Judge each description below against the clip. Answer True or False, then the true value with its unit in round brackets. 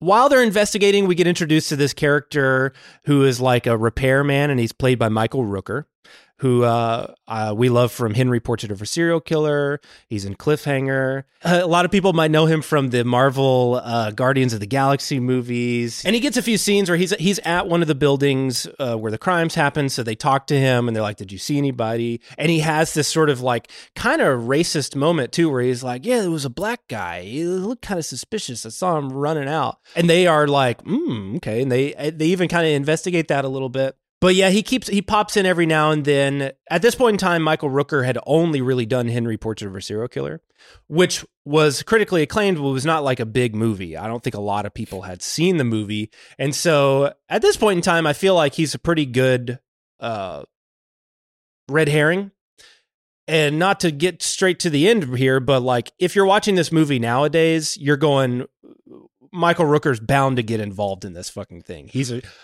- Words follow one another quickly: True (220 wpm)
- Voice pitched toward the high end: False (140 Hz)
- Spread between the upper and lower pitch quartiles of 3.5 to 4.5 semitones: False (5.3 semitones)